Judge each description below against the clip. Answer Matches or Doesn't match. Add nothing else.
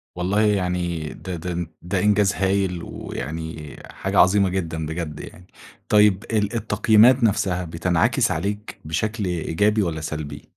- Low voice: Matches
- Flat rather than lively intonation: Doesn't match